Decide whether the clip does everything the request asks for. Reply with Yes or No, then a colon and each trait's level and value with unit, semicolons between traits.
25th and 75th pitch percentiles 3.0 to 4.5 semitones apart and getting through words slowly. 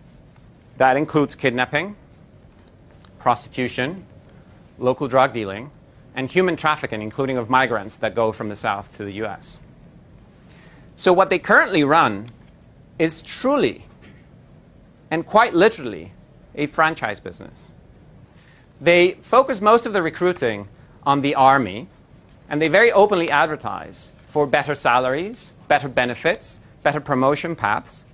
No: average, 4.9 semitones; slow, 120 wpm